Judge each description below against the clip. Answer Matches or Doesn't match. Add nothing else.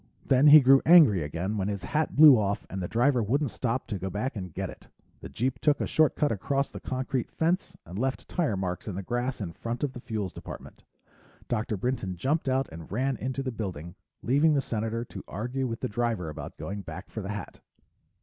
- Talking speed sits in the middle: Doesn't match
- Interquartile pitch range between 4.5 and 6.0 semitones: Matches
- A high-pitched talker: Doesn't match